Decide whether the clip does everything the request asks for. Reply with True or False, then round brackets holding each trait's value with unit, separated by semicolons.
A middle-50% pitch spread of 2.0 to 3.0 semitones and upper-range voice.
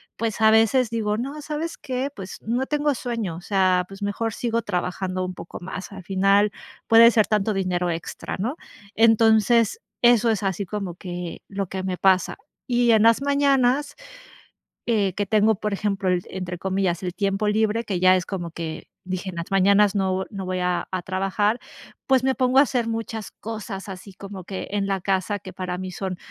False (3.4 semitones; 200 Hz)